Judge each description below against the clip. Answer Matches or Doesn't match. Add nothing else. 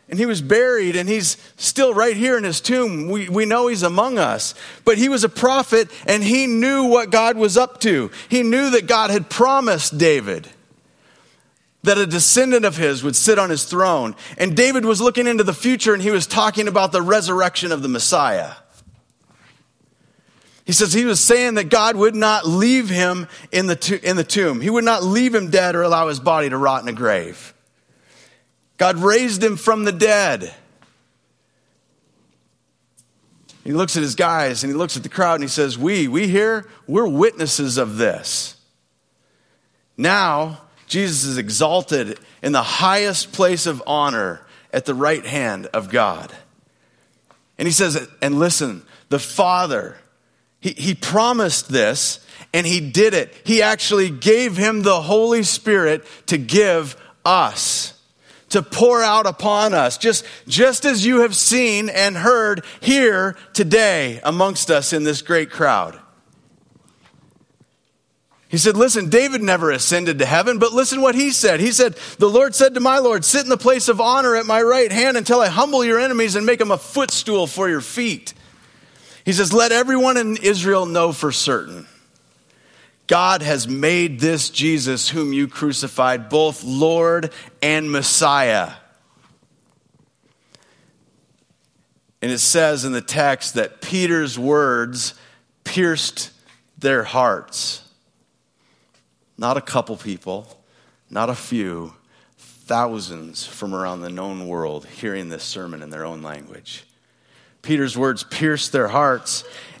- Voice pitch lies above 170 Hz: Matches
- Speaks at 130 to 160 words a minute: Matches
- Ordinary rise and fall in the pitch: Doesn't match